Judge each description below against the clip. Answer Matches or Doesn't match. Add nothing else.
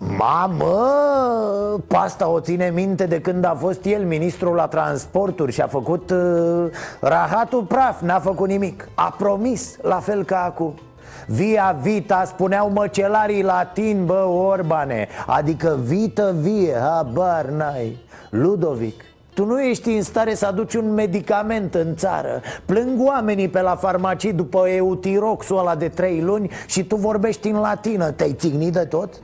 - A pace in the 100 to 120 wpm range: Doesn't match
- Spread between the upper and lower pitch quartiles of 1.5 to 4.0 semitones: Matches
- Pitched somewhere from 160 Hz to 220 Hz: Matches